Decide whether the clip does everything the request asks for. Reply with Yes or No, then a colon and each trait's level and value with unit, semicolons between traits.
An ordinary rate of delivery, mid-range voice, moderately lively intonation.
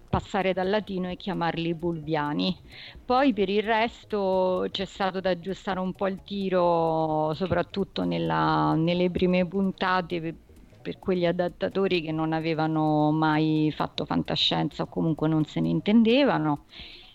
Yes: average, 135 wpm; medium, 180 Hz; average, 3.5 semitones